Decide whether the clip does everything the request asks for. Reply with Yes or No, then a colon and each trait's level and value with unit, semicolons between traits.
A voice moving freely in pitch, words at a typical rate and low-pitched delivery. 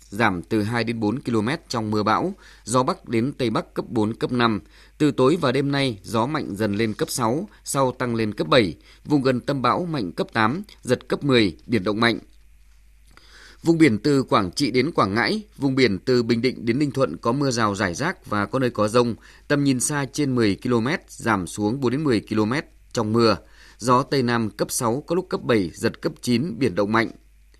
No: average, 4.1 semitones; average, 220 wpm; low, 120 Hz